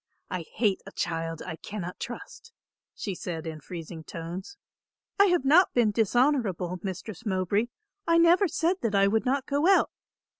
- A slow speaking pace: No, average, 160 wpm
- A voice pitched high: Yes, high, 210 Hz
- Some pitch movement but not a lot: No, wide, 8.2 semitones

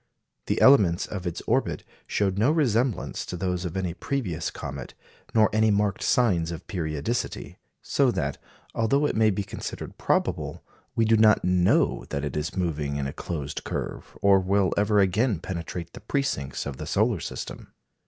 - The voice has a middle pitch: No, very low, 95 Hz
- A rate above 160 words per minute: Yes, average, 170 wpm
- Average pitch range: Yes, average, 4.8 semitones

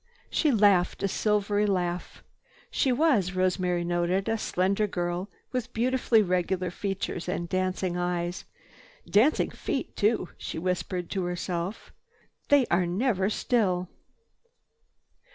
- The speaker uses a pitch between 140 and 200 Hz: Yes, medium, 185 Hz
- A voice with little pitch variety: No, average, 3.0 semitones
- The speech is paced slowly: Yes, slow, 115 wpm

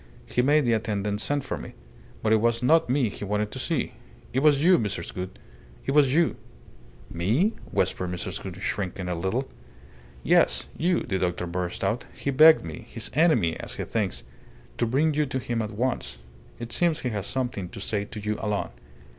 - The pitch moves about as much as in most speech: No, wide, 6.2 semitones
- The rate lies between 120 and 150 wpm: No, average, 195 wpm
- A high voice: No, low, 110 Hz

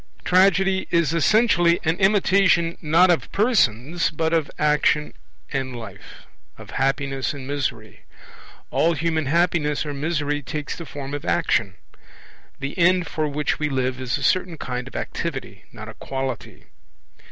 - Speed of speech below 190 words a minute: Yes, average, 145 wpm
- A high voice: No, medium, 150 Hz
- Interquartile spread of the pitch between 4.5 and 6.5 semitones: No, average, 3.9 semitones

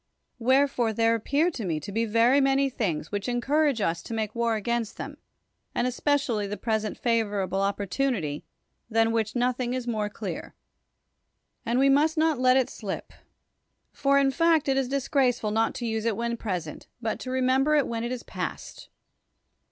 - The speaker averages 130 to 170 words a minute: No, average, 180 wpm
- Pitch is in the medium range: No, high, 235 Hz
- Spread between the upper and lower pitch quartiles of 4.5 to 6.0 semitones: No, average, 3.8 semitones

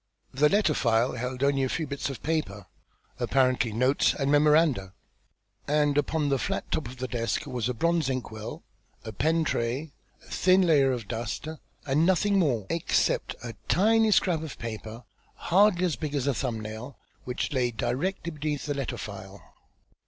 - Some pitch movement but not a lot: Yes, average, 4.9 semitones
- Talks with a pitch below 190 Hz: Yes, medium, 140 Hz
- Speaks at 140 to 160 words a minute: No, average, 175 wpm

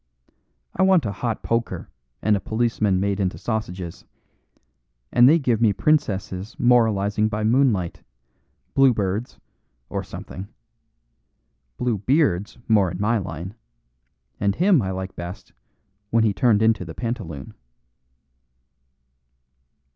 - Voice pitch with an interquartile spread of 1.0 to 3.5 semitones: No, average, 4.0 semitones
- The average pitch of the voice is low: Yes, low, 105 Hz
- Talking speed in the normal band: No, slow, 120 wpm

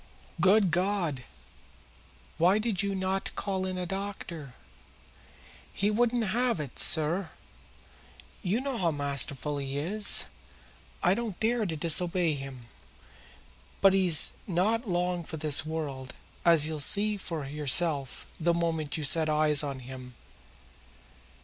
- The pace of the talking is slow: Yes, slow, 130 wpm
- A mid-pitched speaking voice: Yes, medium, 170 Hz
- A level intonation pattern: No, average, 4.7 semitones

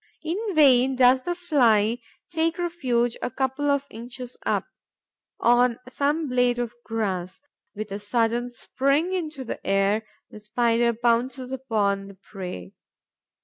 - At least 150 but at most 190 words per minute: No, slow, 135 wpm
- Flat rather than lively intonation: No, average, 3.9 semitones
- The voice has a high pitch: Yes, high, 245 Hz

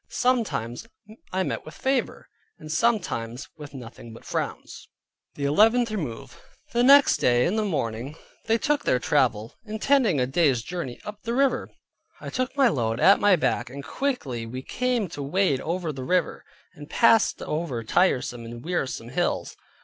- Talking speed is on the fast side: No, average, 165 wpm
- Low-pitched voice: No, medium, 160 Hz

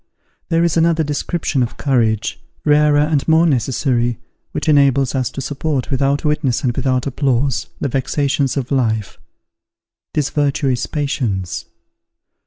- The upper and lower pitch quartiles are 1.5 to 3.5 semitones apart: Yes, average, 2.9 semitones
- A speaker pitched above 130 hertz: Yes, medium, 140 Hz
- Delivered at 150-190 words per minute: No, slow, 135 wpm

